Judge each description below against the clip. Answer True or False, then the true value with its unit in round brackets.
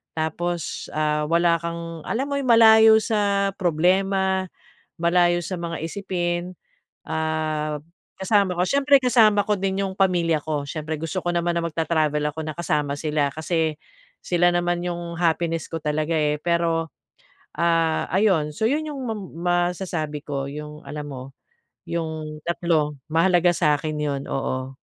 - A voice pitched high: False (170 Hz)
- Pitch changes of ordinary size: True (3.0 semitones)